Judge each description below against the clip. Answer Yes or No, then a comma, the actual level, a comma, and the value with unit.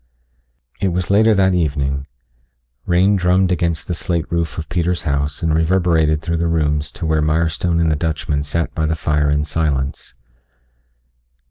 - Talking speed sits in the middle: Yes, average, 160 wpm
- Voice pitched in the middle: No, very low, 80 Hz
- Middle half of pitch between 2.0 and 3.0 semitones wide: Yes, average, 2.7 semitones